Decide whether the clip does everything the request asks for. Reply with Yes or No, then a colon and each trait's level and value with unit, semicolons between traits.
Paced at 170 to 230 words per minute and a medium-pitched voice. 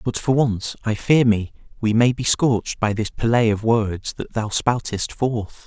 No: average, 200 wpm; low, 110 Hz